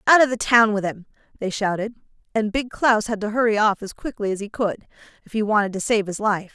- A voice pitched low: No, high, 215 Hz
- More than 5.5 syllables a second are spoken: Yes, 5.9 syllables/s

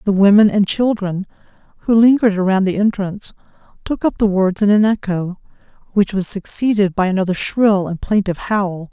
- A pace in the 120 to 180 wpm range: Yes, average, 170 wpm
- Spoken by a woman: Yes, female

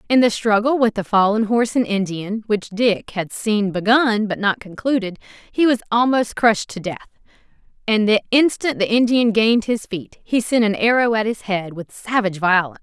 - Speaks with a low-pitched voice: No, high, 215 Hz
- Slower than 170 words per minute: No, average, 190 wpm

